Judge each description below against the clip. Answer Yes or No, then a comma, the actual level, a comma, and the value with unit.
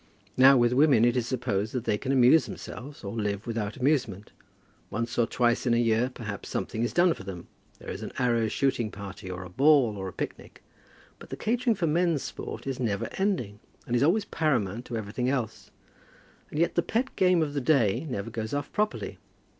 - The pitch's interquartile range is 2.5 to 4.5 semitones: No, average, 5.0 semitones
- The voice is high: No, low, 120 Hz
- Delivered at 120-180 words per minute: No, fast, 205 wpm